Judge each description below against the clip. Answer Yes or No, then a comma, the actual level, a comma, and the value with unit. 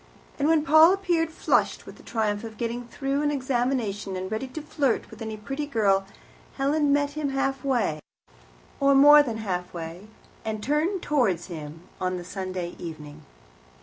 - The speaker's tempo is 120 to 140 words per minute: No, average, 160 wpm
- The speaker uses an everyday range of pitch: No, wide, 6.9 semitones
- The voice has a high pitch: Yes, high, 240 Hz